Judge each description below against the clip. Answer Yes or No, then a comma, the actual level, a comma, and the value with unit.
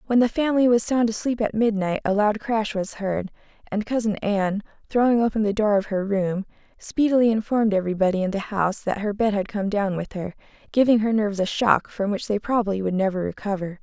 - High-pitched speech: Yes, high, 210 Hz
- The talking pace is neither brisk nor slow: No, fast, 215 wpm